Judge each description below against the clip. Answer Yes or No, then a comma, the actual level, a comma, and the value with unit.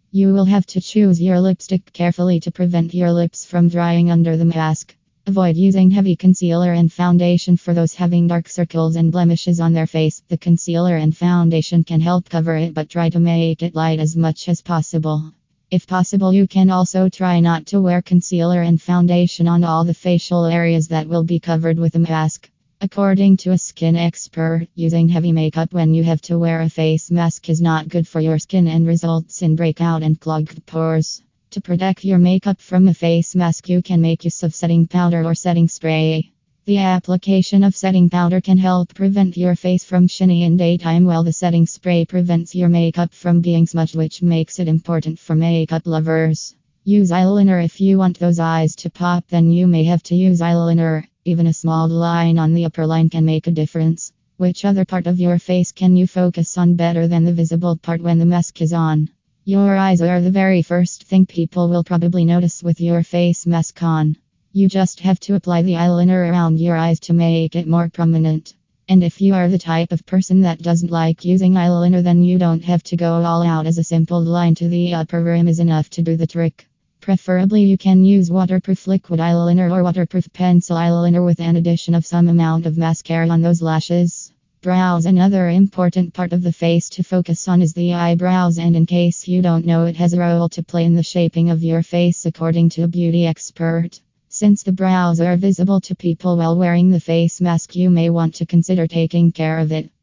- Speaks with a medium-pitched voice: Yes, medium, 170 Hz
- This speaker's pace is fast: Yes, fast, 210 wpm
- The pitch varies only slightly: Yes, narrow, 1.5 semitones